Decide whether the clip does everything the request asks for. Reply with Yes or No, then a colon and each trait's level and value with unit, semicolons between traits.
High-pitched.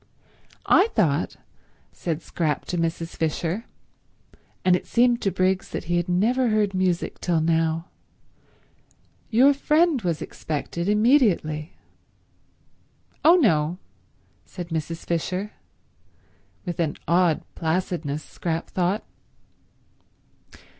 No: medium, 175 Hz